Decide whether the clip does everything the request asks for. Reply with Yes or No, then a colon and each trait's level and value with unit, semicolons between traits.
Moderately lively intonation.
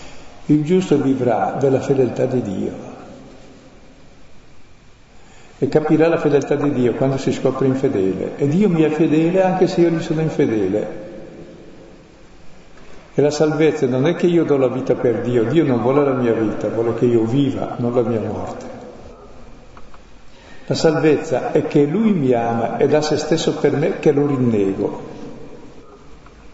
Yes: average, 4.0 semitones